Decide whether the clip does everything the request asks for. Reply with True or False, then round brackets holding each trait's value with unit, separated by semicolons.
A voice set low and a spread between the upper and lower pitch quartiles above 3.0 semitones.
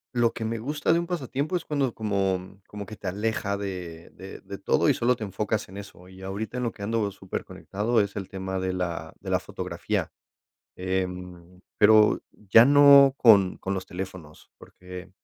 True (100 Hz; 3.5 semitones)